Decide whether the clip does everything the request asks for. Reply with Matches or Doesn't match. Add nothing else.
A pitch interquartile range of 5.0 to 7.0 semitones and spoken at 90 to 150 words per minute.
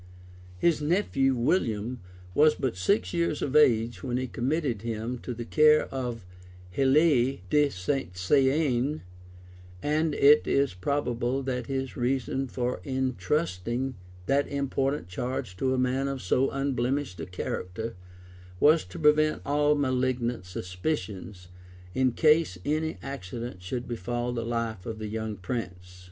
Doesn't match